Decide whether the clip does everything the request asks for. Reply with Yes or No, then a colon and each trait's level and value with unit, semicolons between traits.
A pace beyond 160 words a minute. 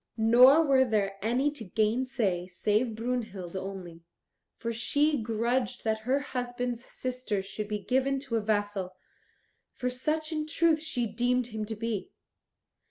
No: average, 145 wpm